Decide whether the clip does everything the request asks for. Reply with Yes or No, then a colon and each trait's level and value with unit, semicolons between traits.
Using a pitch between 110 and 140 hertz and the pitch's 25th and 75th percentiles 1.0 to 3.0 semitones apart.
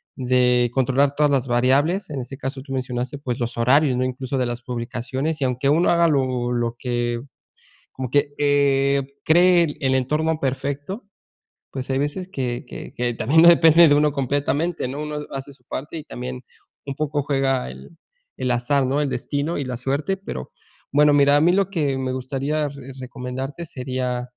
Yes: low, 135 Hz; average, 2.7 semitones